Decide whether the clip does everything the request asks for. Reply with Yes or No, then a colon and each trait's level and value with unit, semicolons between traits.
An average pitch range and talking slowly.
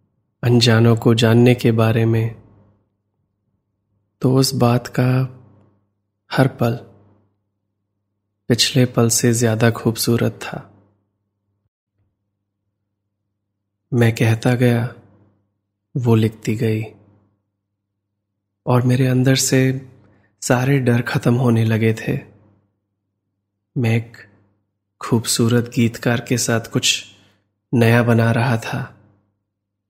Yes: average, 3.0 semitones; slow, 90 wpm